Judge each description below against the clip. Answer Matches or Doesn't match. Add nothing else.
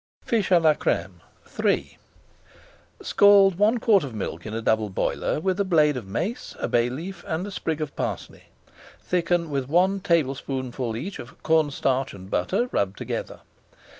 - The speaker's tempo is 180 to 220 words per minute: Doesn't match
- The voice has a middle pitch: Matches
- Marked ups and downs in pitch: Matches